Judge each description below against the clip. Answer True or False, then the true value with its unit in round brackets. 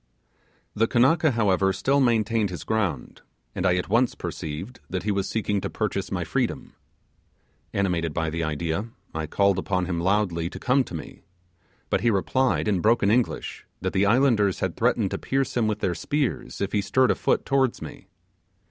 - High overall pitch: False (100 Hz)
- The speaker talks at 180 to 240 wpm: True (185 wpm)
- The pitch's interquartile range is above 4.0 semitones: True (4.6 semitones)